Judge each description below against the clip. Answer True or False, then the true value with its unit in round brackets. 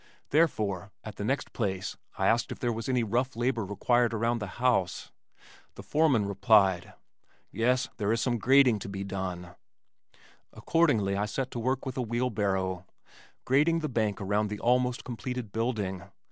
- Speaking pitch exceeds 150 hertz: False (115 Hz)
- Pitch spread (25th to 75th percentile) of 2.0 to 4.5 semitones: True (4.0 semitones)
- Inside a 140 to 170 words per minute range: True (160 wpm)